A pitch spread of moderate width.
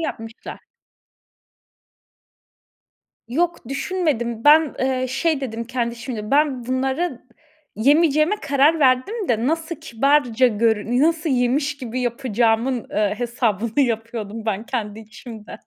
Yes: average, 4.2 semitones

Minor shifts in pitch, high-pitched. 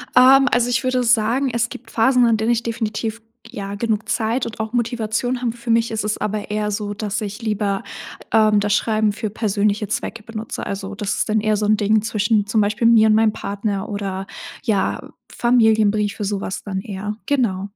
Yes: narrow, 1.9 semitones; high, 215 Hz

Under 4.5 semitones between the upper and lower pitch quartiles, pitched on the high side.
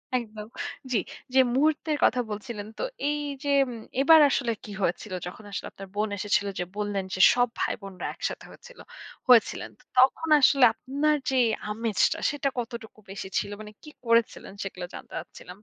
No: average, 4.8 semitones; high, 230 Hz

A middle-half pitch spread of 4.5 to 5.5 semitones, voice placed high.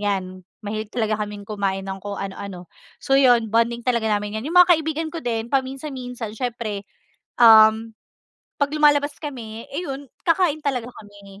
Yes: average, 4.8 semitones; high, 230 Hz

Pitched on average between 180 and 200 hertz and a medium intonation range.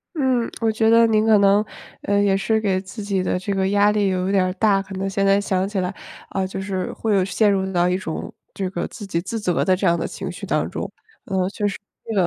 No: high, 195 Hz; narrow, 1.8 semitones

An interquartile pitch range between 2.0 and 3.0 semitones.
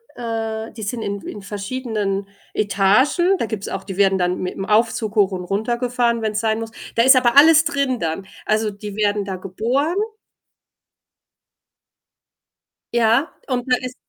No: average, 3.5 semitones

